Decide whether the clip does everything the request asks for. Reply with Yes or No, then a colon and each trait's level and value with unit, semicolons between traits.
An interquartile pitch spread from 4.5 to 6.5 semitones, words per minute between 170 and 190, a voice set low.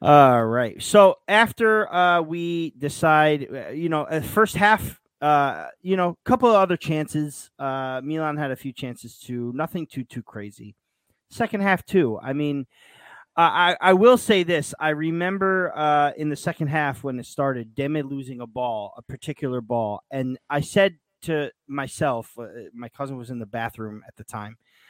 No: wide, 5.4 semitones; average, 175 wpm; medium, 145 Hz